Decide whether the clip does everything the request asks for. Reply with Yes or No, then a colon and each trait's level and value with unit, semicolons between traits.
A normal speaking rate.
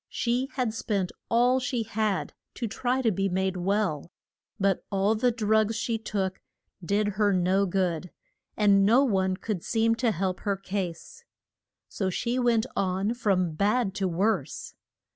Yes: average, 155 wpm